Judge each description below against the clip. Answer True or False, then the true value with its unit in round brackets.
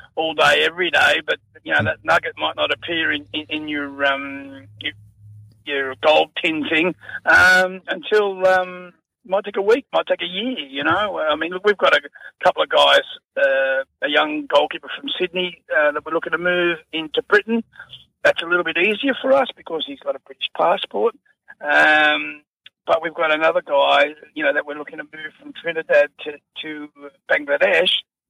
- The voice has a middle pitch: True (170 Hz)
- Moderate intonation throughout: False (7.6 semitones)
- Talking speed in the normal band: True (195 wpm)